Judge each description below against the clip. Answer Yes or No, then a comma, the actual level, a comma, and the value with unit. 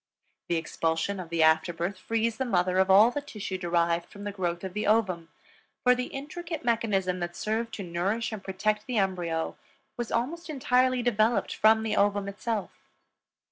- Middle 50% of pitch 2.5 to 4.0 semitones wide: No, average, 4.6 semitones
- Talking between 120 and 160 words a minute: No, average, 180 wpm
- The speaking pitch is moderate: No, high, 205 Hz